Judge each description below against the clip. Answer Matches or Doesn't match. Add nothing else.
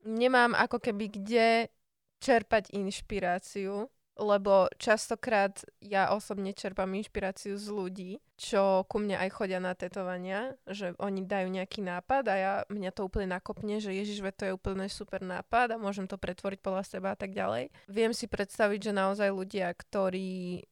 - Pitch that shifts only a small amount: Matches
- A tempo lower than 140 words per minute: Doesn't match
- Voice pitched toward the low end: Doesn't match